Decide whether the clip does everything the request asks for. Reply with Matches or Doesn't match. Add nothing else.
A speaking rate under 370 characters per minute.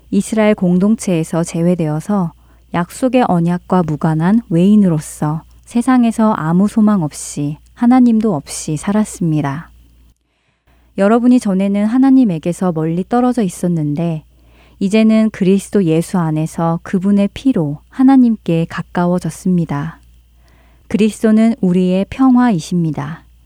Matches